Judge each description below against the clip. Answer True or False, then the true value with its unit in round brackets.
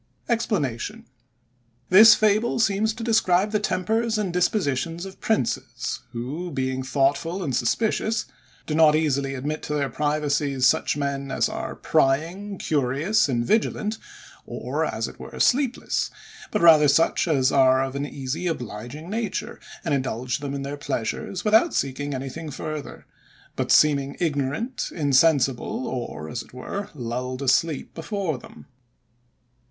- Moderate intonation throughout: False (6.5 semitones)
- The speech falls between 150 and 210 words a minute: False (135 wpm)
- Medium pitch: True (145 Hz)